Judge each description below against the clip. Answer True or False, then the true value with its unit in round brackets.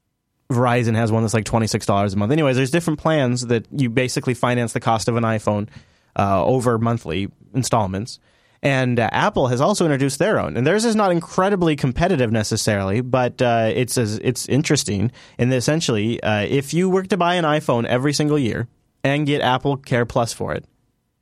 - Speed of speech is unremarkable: True (185 wpm)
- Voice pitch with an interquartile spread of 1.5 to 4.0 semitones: False (4.4 semitones)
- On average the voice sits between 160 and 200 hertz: False (125 Hz)